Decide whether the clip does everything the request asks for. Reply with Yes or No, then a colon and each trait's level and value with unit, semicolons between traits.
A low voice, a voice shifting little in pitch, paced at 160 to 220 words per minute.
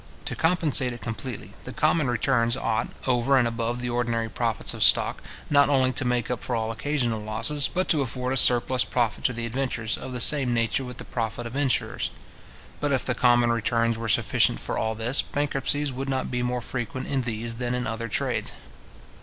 Yes: low, 125 Hz; narrow, 2.3 semitones; fast, 205 wpm